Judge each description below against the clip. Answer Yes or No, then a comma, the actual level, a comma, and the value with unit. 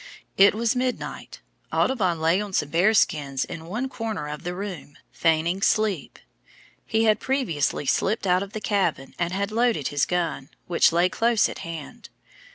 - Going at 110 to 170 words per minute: Yes, average, 165 wpm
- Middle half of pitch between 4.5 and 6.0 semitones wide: Yes, average, 4.8 semitones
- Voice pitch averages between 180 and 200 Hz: Yes, medium, 185 Hz